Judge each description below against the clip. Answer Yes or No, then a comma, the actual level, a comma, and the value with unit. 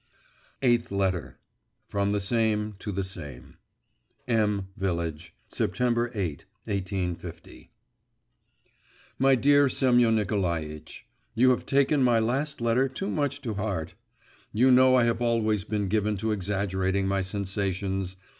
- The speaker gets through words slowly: Yes, slow, 125 wpm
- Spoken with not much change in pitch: No, average, 4.1 semitones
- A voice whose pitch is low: Yes, low, 105 Hz